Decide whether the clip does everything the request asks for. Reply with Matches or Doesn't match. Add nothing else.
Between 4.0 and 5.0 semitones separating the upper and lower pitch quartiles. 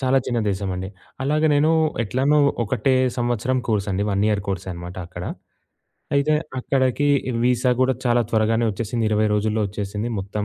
Matches